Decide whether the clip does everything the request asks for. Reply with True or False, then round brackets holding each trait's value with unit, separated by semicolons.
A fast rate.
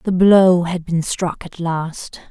False (180 wpm)